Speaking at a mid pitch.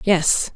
Yes: medium, 180 Hz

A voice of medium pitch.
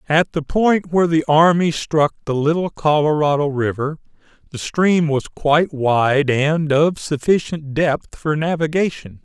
Yes: medium, 155 Hz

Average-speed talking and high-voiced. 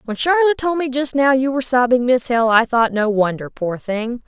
No: fast, 240 wpm; very high, 250 Hz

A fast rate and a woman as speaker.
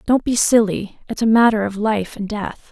Yes: fast, 220 wpm; female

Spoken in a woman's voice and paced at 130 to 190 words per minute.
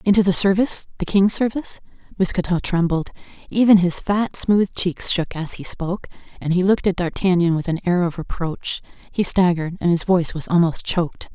Yes: female; average, 180 wpm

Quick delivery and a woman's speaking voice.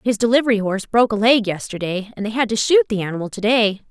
Yes: fast, 245 wpm; female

